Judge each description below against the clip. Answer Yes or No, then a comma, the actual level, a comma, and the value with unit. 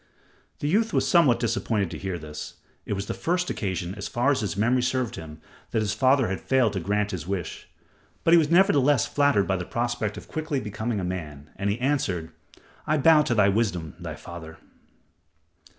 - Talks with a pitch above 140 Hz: No, low, 110 Hz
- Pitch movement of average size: No, wide, 6.3 semitones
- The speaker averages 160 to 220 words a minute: Yes, average, 200 wpm